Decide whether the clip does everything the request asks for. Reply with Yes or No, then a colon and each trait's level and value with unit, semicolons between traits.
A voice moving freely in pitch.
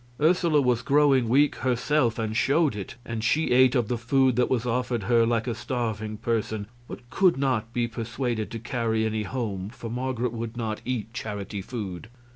No: average, 2.7 semitones